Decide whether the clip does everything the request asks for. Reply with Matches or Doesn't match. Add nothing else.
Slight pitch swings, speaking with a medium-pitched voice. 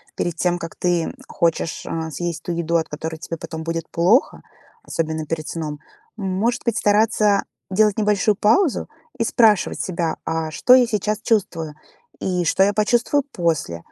Doesn't match